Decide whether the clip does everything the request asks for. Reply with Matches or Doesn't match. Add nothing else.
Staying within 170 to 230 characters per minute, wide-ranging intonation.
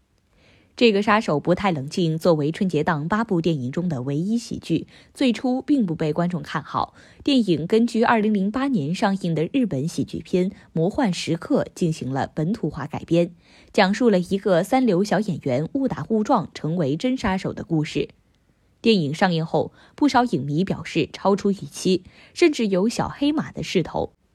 Doesn't match